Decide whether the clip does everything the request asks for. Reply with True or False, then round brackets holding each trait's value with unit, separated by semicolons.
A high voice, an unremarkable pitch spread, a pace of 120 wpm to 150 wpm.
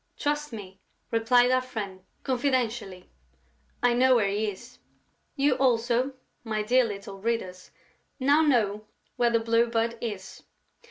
True (230 Hz; 3.3 semitones; 140 wpm)